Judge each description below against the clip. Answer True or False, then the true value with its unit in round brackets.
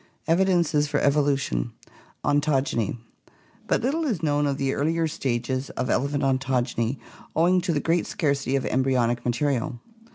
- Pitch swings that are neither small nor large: True (3.5 semitones)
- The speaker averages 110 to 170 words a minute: True (135 wpm)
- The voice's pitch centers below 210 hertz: True (140 Hz)